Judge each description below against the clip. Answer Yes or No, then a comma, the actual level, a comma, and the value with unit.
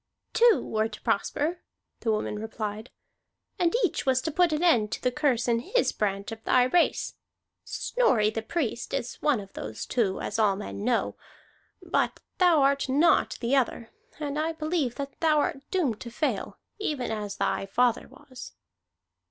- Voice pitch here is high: Yes, very high, 255 Hz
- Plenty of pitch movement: Yes, wide, 5.7 semitones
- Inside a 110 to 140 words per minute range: No, average, 170 wpm